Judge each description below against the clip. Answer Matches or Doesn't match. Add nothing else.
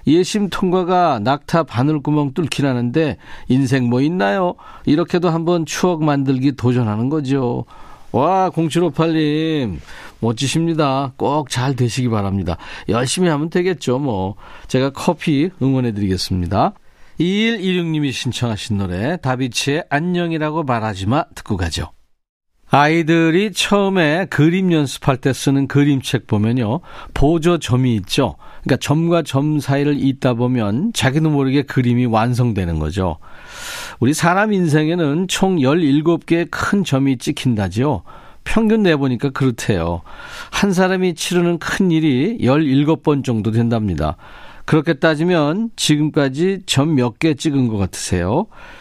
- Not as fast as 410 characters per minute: Matches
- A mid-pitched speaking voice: Matches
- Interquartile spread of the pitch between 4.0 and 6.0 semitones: Matches